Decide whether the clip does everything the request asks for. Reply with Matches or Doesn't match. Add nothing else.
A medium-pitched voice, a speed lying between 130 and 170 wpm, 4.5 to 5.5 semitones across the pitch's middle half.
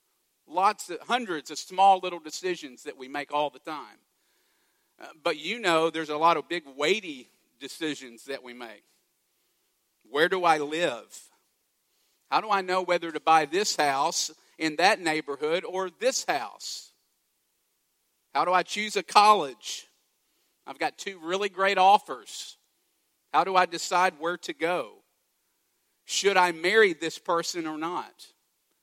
Matches